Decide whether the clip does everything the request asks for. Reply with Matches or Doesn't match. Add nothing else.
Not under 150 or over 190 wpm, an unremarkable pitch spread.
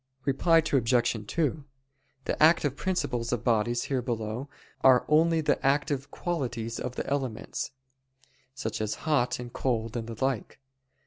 Doesn't match